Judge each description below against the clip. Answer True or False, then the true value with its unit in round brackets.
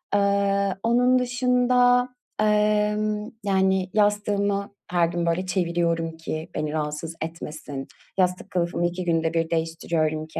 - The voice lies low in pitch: False (185 Hz)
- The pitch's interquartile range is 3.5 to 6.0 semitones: True (4.1 semitones)